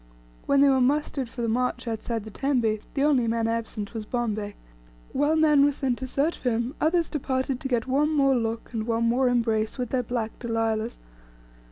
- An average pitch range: Yes, average, 3.3 semitones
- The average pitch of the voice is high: Yes, high, 245 Hz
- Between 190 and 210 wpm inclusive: Yes, average, 200 wpm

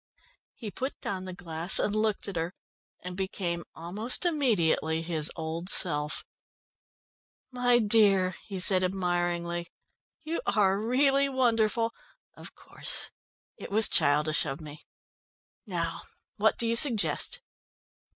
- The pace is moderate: No, slow, 120 wpm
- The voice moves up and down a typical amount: Yes, average, 4.9 semitones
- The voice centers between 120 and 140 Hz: No, high, 190 Hz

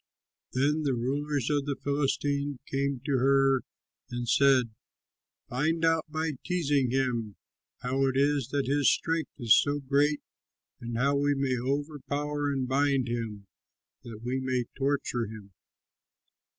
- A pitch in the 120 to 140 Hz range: Yes, low, 135 Hz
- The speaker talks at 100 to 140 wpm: Yes, slow, 135 wpm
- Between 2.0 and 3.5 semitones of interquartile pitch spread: Yes, narrow, 2.4 semitones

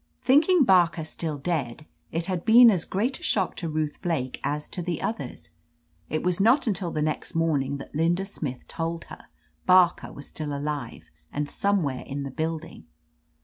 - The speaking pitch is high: No, medium, 165 Hz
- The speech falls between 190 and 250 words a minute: No, average, 175 wpm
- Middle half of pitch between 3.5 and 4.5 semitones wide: Yes, average, 4.1 semitones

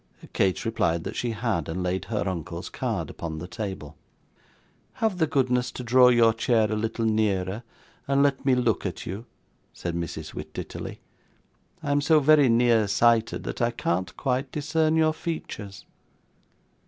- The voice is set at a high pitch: No, low, 115 Hz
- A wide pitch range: Yes, wide, 5.7 semitones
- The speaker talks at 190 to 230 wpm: No, average, 155 wpm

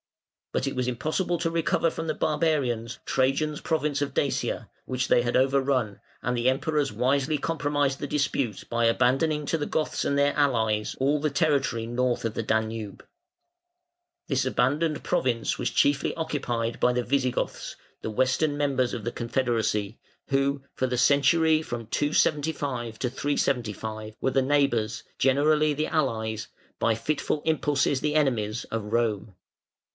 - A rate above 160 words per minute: No, average, 150 wpm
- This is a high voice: No, low, 135 Hz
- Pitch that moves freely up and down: No, average, 3.8 semitones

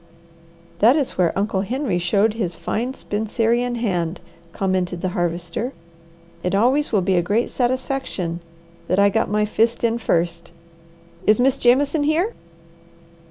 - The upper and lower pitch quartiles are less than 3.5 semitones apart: No, average, 5.3 semitones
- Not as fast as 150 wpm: Yes, average, 140 wpm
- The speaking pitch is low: No, high, 215 Hz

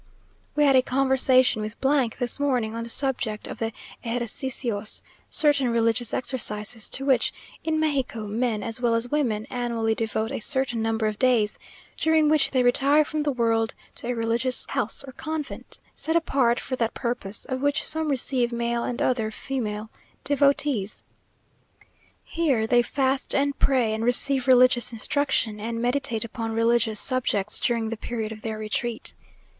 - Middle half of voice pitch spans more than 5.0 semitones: No, average, 3.3 semitones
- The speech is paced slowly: No, average, 160 wpm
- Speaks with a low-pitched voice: No, high, 240 Hz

